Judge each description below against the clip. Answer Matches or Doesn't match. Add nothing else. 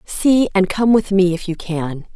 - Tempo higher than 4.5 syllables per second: Doesn't match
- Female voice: Matches